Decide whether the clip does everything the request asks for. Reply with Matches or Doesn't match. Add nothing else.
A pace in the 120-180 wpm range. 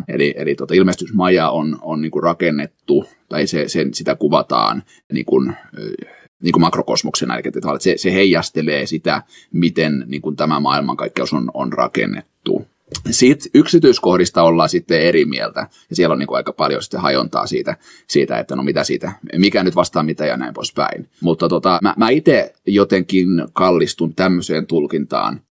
Matches